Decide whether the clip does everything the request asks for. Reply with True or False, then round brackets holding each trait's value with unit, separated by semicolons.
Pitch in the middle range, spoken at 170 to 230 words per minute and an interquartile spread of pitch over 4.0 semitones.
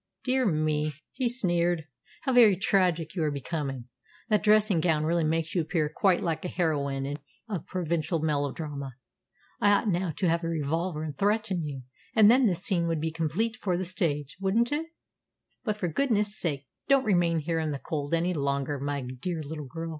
True (165 Hz; 185 wpm; 4.5 semitones)